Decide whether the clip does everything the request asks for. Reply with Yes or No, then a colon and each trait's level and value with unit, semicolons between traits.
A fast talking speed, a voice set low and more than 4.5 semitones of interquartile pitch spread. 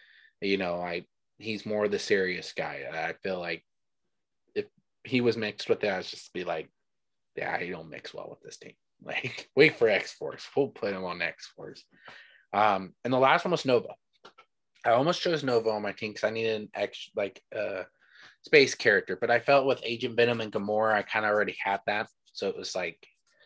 Yes: fast, 210 wpm; low, 115 Hz; average, 5.0 semitones